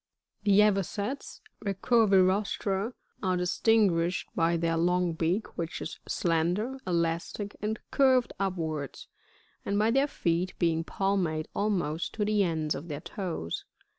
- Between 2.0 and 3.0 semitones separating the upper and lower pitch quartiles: No, average, 3.8 semitones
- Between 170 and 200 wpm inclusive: No, slow, 135 wpm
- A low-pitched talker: No, medium, 185 Hz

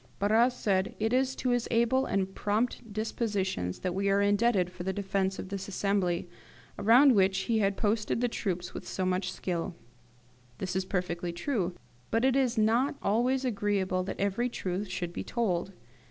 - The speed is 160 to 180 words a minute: Yes, average, 175 wpm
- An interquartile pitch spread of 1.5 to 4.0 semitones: Yes, average, 3.7 semitones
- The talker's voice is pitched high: Yes, high, 200 Hz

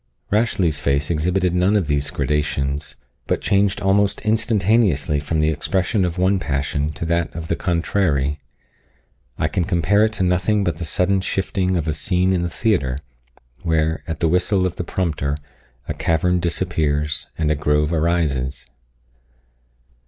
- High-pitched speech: No, very low, 85 Hz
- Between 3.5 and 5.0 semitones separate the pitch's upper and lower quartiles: Yes, average, 3.8 semitones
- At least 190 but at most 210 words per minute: No, average, 155 wpm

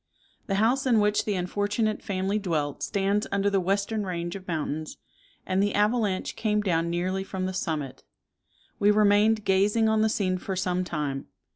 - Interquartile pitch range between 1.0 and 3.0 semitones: Yes, narrow, 2.5 semitones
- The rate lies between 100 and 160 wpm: No, average, 170 wpm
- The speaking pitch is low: No, high, 195 Hz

